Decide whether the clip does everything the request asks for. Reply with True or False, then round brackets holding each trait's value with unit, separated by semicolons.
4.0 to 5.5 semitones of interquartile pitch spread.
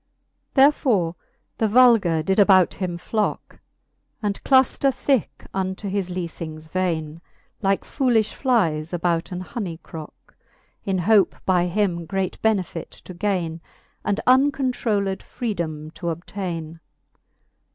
True (4.3 semitones)